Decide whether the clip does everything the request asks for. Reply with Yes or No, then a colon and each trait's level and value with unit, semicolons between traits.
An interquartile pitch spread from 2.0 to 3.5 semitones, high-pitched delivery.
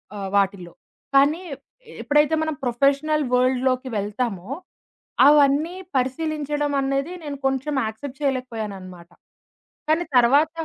No: average, 4.0 semitones; very high, 275 Hz